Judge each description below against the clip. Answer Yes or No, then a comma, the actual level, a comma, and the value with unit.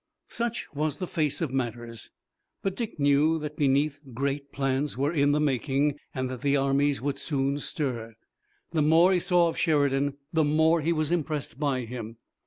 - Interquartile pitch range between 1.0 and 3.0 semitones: Yes, narrow, 2.6 semitones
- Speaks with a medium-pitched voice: Yes, medium, 145 Hz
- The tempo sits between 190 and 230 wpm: No, average, 180 wpm